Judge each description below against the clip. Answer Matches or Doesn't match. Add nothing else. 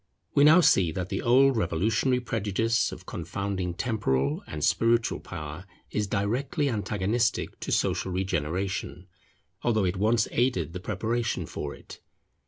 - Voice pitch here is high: Doesn't match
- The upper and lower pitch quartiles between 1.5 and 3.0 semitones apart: Doesn't match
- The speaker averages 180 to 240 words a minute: Doesn't match